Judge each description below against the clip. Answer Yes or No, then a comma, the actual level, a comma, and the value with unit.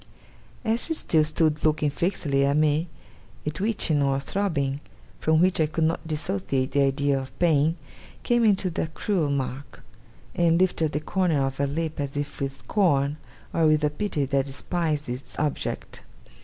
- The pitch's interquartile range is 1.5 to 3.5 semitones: Yes, average, 3.2 semitones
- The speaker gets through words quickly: No, average, 170 wpm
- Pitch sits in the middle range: Yes, medium, 150 Hz